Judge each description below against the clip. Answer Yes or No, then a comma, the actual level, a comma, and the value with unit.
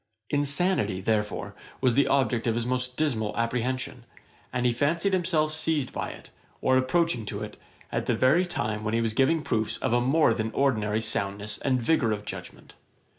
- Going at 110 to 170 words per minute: No, average, 180 wpm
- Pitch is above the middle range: No, low, 125 Hz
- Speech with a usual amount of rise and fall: Yes, average, 4.7 semitones